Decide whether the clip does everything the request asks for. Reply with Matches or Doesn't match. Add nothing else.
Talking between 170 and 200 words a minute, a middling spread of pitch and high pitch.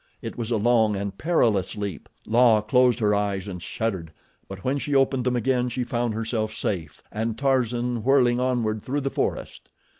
Doesn't match